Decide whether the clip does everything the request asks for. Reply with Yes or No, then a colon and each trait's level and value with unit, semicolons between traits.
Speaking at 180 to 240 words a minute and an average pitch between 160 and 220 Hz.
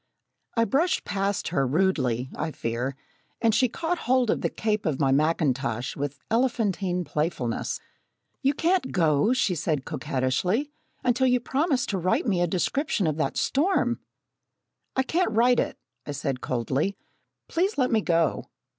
No: average, 155 wpm; high, 190 Hz